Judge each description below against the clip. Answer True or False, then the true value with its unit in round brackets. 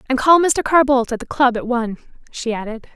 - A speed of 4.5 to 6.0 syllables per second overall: True (5.9 syllables/s)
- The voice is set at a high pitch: True (255 Hz)